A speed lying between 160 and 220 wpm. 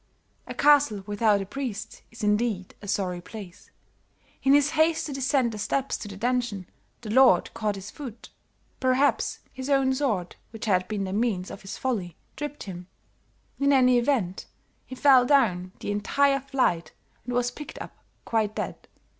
Yes: average, 170 wpm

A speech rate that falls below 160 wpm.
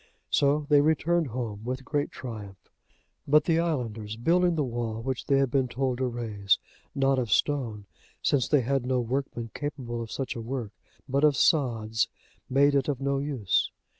No: average, 175 wpm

